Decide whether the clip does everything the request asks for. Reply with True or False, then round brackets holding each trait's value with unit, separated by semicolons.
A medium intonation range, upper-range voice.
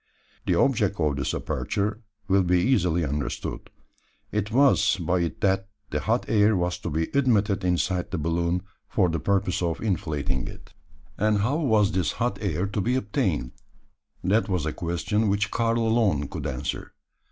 False (3.8 semitones; 95 Hz)